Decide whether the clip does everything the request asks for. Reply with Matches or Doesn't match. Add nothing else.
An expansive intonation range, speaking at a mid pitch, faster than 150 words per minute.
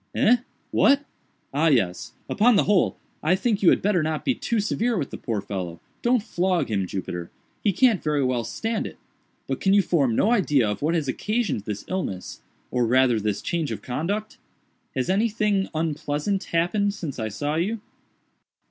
Matches